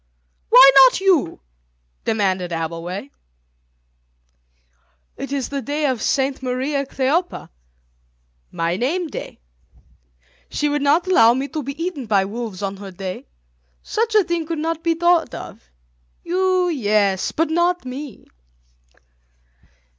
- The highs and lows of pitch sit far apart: Yes, wide, 7.9 semitones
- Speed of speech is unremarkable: No, slow, 125 wpm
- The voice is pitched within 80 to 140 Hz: No, very high, 275 Hz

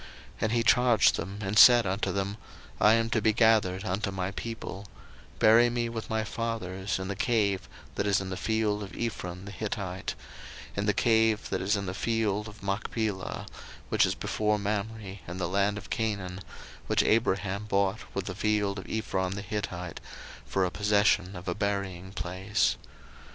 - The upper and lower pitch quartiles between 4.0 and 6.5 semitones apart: No, narrow, 2.5 semitones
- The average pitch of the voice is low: Yes, low, 100 Hz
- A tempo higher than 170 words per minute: Yes, average, 180 wpm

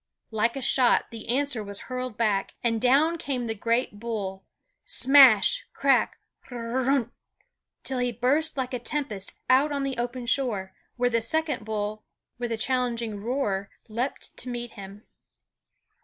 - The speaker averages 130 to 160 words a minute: Yes, average, 155 wpm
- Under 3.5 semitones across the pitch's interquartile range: Yes, average, 3.1 semitones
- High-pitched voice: Yes, high, 240 Hz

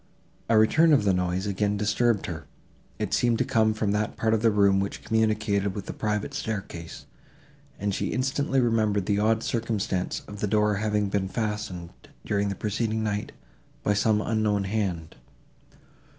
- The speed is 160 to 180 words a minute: Yes, average, 165 wpm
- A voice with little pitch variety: Yes, narrow, 1.7 semitones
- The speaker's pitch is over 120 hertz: No, low, 105 Hz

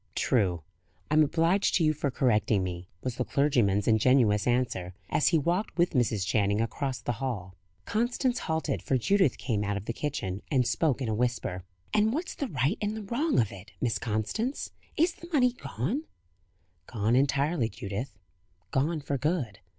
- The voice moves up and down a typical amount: No, wide, 7.7 semitones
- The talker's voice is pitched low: Yes, low, 130 Hz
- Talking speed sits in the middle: Yes, average, 175 wpm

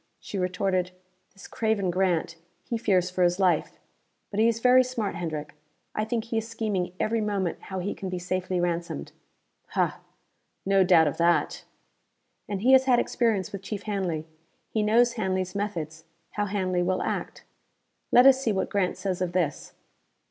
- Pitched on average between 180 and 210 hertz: Yes, high, 190 Hz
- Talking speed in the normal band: Yes, average, 170 wpm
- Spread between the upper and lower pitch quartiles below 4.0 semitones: Yes, average, 3.4 semitones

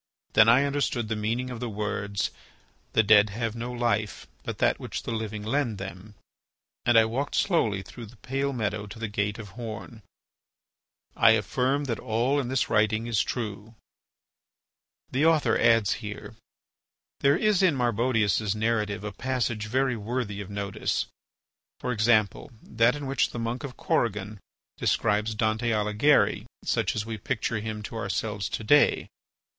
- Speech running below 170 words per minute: Yes, average, 150 wpm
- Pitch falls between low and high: No, low, 110 Hz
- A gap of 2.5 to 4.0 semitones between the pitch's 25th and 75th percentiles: Yes, average, 2.8 semitones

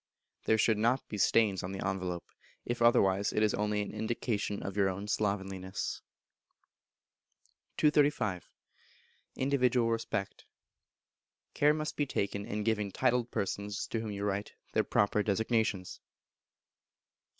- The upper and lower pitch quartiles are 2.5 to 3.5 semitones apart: Yes, average, 2.9 semitones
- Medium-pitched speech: No, low, 105 Hz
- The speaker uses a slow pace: Yes, slow, 130 wpm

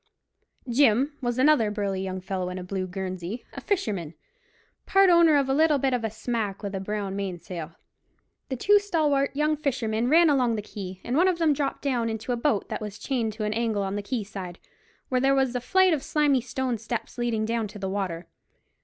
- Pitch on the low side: No, high, 230 Hz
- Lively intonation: Yes, wide, 5.7 semitones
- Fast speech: Yes, fast, 215 wpm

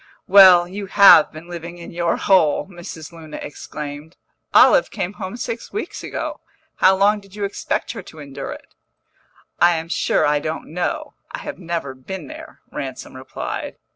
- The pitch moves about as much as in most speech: Yes, average, 4.0 semitones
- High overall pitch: No, medium, 175 Hz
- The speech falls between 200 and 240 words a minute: No, average, 170 wpm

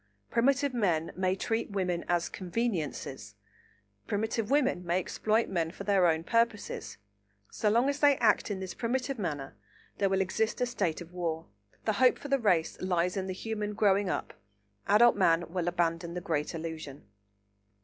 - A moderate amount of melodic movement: Yes, average, 4.9 semitones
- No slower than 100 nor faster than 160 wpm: No, average, 170 wpm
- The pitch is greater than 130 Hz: Yes, high, 190 Hz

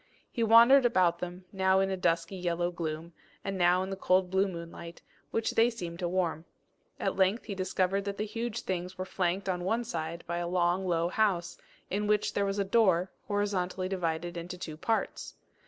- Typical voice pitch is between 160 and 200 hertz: Yes, medium, 185 Hz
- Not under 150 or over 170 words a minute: No, average, 195 wpm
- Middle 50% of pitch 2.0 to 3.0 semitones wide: Yes, narrow, 2.4 semitones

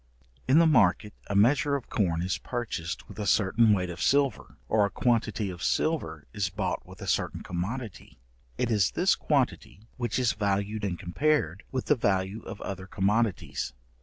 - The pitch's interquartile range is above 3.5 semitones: Yes, average, 4.2 semitones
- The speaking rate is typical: Yes, average, 175 wpm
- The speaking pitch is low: Yes, low, 105 Hz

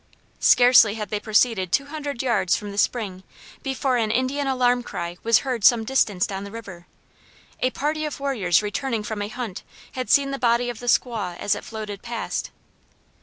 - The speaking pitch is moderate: No, high, 230 Hz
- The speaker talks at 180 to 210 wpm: Yes, average, 185 wpm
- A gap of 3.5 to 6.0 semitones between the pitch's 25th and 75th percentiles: Yes, average, 3.9 semitones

